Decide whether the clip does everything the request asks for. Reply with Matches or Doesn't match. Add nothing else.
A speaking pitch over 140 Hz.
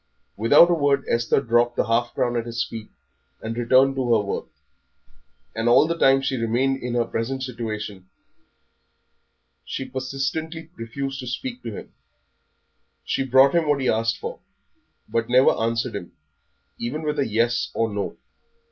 Doesn't match